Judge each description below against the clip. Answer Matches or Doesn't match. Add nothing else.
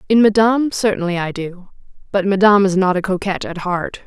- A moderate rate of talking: Matches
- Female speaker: Matches